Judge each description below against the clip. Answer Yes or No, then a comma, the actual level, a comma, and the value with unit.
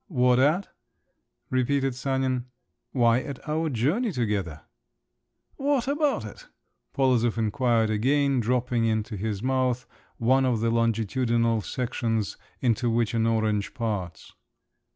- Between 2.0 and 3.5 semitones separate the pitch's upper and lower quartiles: Yes, average, 2.9 semitones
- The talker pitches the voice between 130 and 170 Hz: No, low, 120 Hz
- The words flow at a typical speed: No, slow, 115 wpm